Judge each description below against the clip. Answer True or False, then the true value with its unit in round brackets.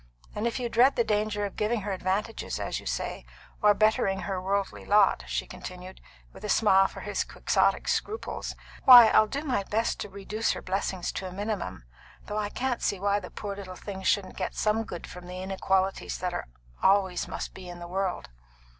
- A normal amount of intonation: False (2.3 semitones)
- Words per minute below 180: False (200 wpm)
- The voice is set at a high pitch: True (200 Hz)